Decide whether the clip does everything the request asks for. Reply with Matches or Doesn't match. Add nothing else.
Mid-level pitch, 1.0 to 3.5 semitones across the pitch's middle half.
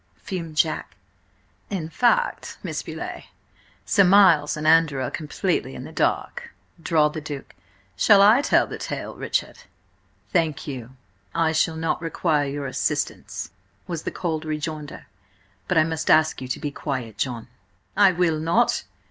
Matches